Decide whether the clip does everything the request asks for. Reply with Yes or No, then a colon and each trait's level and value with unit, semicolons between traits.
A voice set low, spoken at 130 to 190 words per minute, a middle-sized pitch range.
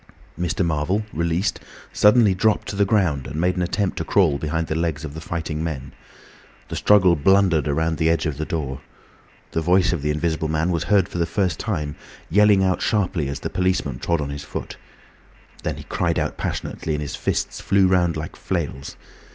No: very low, 85 Hz; average, 200 wpm; average, 3.5 semitones